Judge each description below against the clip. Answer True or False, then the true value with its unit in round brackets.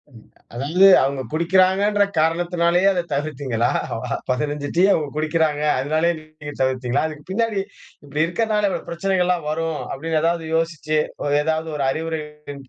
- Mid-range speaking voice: True (160 Hz)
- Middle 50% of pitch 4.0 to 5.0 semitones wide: False (3.2 semitones)